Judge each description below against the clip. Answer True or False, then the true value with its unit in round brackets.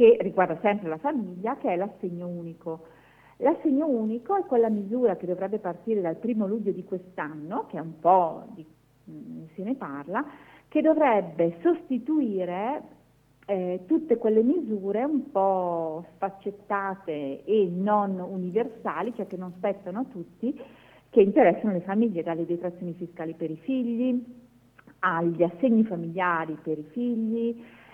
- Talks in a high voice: True (195 Hz)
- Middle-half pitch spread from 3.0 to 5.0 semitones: False (5.5 semitones)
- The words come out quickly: False (140 wpm)